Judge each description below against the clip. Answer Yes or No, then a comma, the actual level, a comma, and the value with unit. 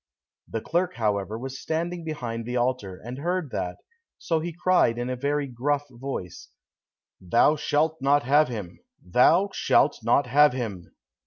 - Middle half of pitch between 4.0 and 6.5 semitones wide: Yes, average, 5.1 semitones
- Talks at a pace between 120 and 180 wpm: Yes, average, 155 wpm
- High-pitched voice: No, low, 130 Hz